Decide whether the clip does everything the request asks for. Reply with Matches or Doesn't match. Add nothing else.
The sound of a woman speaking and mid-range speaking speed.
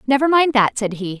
Doesn't match